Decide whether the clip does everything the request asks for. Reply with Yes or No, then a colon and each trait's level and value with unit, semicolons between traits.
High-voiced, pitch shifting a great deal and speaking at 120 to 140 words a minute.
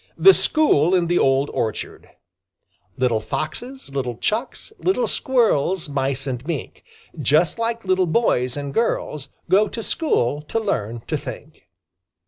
No: medium, 155 Hz; wide, 9.0 semitones; slow, 135 wpm